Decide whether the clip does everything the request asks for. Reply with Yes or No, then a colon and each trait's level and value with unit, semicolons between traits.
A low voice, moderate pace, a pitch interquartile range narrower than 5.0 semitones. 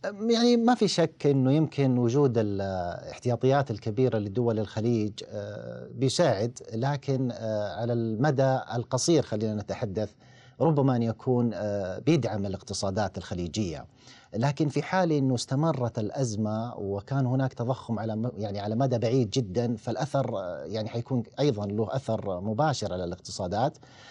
Yes: low, 120 Hz; average, 120 wpm; average, 4.0 semitones